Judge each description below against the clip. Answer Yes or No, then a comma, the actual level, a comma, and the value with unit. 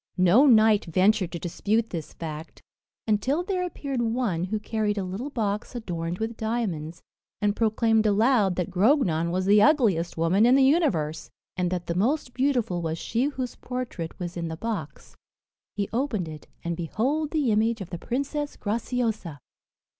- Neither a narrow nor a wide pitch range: No, wide, 5.9 semitones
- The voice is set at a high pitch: Yes, high, 215 Hz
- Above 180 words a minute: No, average, 165 wpm